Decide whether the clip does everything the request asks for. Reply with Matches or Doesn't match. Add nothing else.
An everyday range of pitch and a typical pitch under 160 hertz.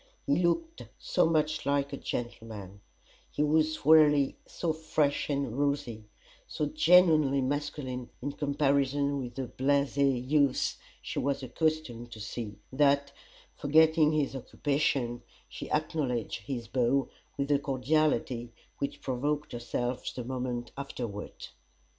Matches